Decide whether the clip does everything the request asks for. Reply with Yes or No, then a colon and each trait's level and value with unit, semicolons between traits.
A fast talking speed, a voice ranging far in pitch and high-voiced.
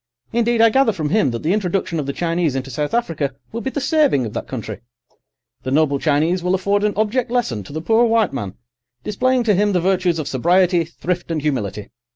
No: fast, 215 wpm; wide, 7.1 semitones; medium, 175 Hz